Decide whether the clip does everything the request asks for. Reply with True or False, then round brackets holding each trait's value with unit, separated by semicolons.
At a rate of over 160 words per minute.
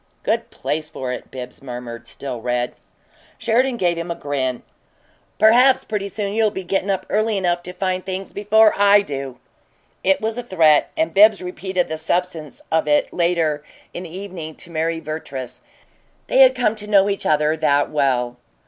True (175 wpm)